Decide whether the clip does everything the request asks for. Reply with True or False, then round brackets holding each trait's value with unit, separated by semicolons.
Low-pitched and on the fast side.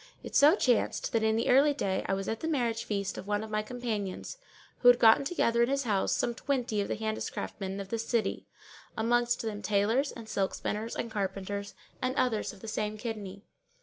False (220 Hz; 210 wpm)